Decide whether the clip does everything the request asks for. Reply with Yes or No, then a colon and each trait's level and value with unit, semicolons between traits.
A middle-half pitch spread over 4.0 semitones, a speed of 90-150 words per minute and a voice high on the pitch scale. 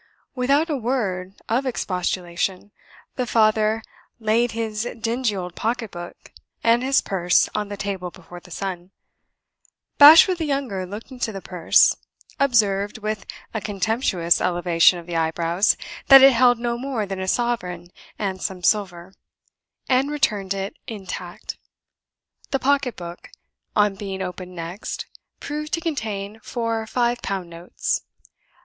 Yes: average, 4.8 semitones; average, 140 wpm; high, 210 Hz